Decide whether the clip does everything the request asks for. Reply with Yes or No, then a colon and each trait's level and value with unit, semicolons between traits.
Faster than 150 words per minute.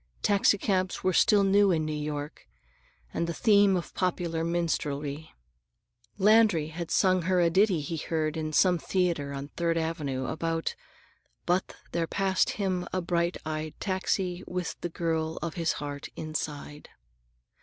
No: average, 145 wpm